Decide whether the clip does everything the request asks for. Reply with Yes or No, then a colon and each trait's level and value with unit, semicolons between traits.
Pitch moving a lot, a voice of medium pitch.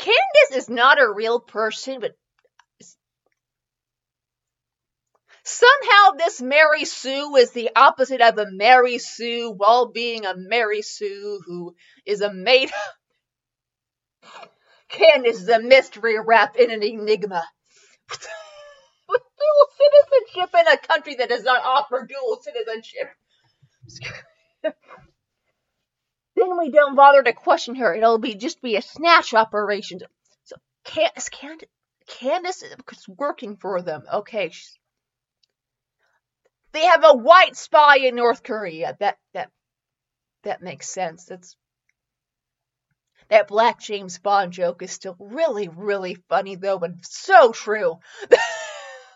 No: wide, 6.7 semitones; high, 245 Hz